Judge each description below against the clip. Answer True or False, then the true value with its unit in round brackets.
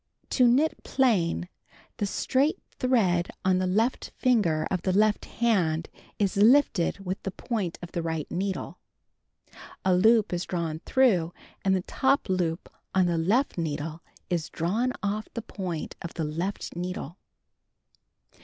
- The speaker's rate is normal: True (155 wpm)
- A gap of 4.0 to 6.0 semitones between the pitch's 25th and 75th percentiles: True (4.7 semitones)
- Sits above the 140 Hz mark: True (185 Hz)